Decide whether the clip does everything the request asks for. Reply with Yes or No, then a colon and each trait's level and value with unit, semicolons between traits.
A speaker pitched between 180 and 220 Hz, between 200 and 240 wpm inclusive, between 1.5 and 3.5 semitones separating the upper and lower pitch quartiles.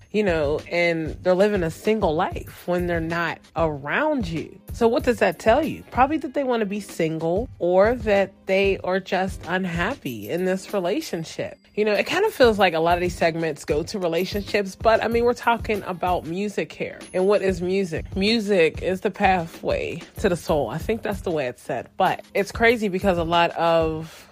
No: high, 190 Hz; fast, 205 wpm; average, 4.0 semitones